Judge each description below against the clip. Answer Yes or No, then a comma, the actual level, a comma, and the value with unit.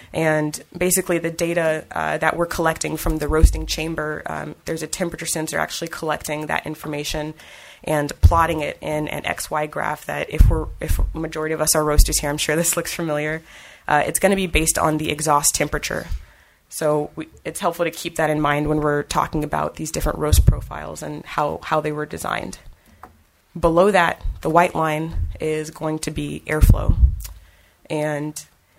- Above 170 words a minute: Yes, average, 185 wpm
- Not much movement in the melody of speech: Yes, narrow, 1.8 semitones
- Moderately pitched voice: Yes, medium, 155 Hz